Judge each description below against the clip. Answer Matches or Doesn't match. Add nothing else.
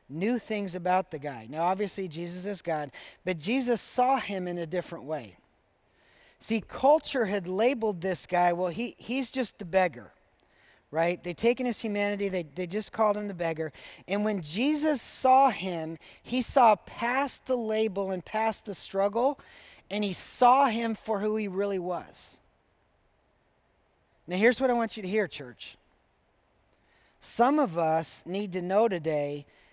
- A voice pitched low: Doesn't match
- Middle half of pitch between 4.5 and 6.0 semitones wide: Matches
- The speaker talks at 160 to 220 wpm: Matches